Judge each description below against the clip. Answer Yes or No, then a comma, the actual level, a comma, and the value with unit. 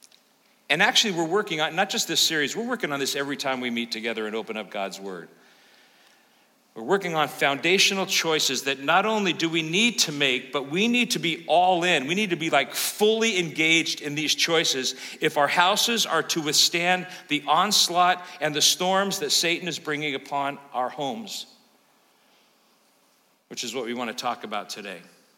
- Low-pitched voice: No, medium, 165 Hz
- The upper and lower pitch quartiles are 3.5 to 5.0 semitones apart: Yes, average, 4.7 semitones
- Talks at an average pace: Yes, average, 190 wpm